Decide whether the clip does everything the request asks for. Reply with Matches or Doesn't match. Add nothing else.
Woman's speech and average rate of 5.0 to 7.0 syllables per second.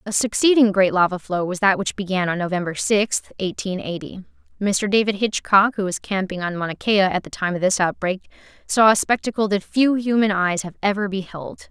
Matches